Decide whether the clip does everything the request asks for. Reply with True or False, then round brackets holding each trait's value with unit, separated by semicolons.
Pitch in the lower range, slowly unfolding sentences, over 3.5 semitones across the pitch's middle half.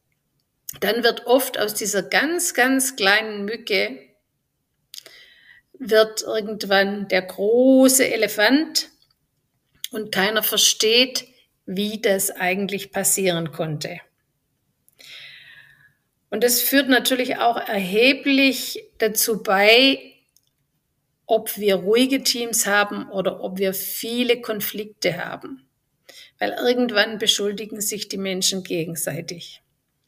False (210 Hz; 95 wpm; 4.2 semitones)